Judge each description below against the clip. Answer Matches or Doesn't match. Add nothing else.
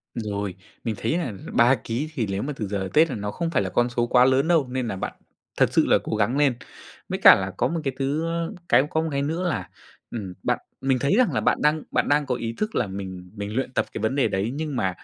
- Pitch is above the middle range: Doesn't match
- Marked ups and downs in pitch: Matches